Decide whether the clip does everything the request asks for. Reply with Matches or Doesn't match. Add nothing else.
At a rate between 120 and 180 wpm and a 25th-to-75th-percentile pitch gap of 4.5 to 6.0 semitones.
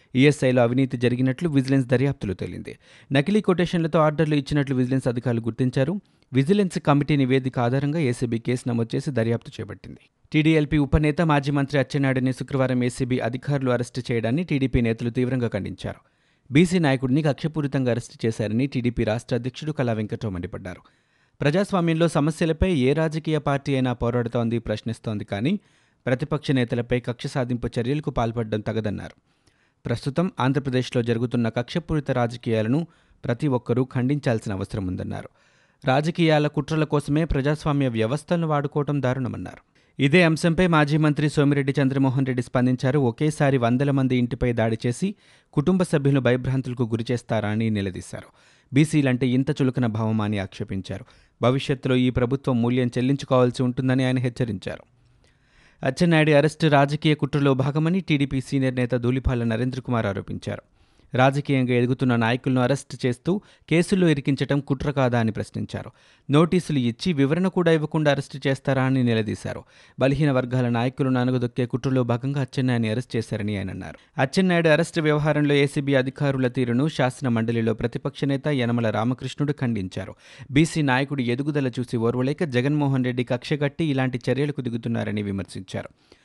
Doesn't match